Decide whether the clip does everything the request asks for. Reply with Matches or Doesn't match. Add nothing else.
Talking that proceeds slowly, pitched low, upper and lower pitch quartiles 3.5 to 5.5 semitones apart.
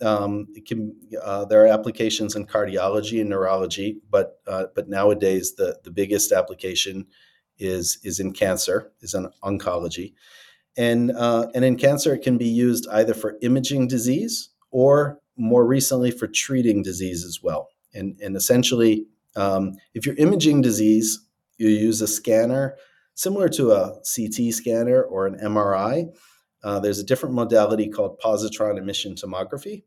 Doesn't match